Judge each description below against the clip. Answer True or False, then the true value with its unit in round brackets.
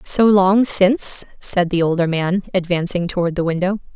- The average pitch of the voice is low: False (185 Hz)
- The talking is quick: False (165 wpm)